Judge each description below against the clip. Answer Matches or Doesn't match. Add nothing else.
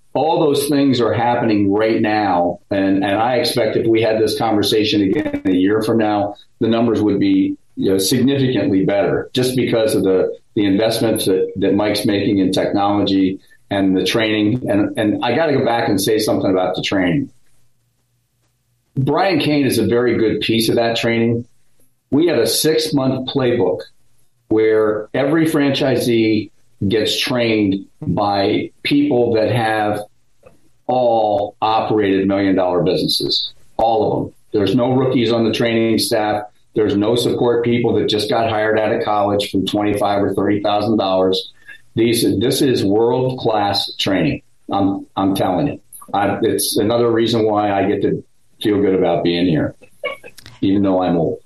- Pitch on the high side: Doesn't match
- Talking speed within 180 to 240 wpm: Doesn't match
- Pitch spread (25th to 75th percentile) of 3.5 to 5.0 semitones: Doesn't match